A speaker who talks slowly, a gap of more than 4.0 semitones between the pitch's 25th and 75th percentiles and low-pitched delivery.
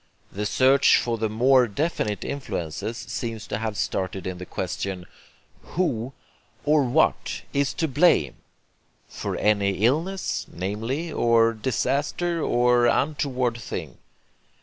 Yes: slow, 120 wpm; average, 5.0 semitones; low, 120 Hz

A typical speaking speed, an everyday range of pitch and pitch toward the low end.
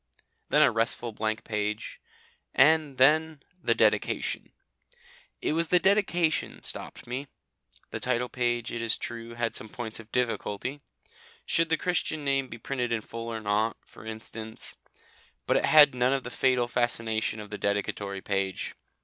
Yes: average, 160 wpm; average, 3.8 semitones; low, 120 Hz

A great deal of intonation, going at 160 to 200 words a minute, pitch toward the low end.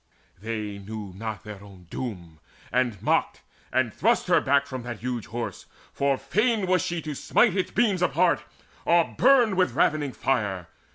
Yes: wide, 8.5 semitones; average, 165 wpm; low, 130 Hz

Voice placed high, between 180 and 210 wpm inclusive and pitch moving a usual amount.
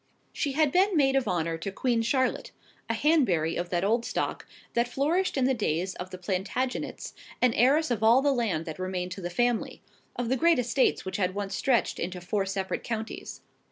No: high, 230 Hz; average, 200 wpm; wide, 6.1 semitones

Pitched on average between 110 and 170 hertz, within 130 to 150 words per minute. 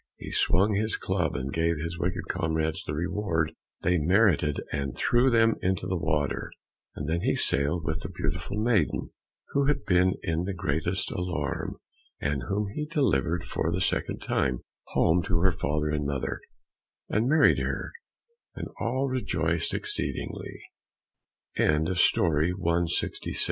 No: very low, 85 Hz; average, 140 wpm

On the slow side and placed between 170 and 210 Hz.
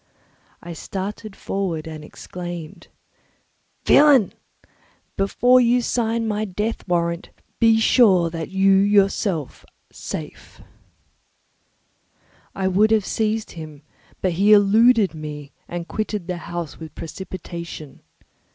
Yes: slow, 110 wpm; high, 190 Hz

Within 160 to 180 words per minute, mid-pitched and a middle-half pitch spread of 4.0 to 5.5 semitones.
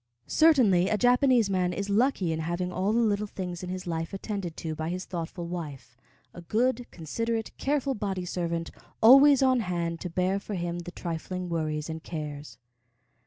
Yes: average, 175 wpm; medium, 180 Hz; average, 4.3 semitones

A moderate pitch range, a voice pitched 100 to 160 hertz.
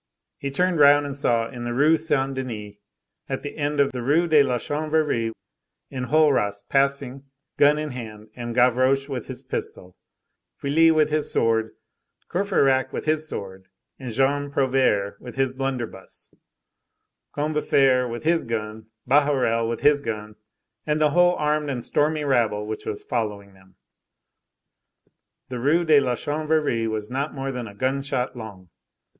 Yes: average, 4.3 semitones; low, 135 Hz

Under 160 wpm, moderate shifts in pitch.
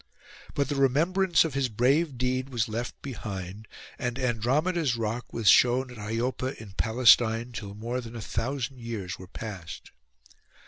Yes: average, 150 wpm; average, 3.2 semitones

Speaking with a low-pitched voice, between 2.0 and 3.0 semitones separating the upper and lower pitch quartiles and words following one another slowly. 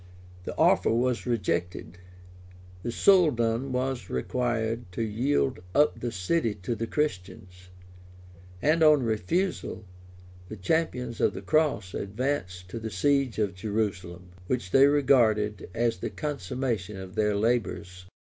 No: low, 115 Hz; wide, 5.5 semitones; slow, 130 wpm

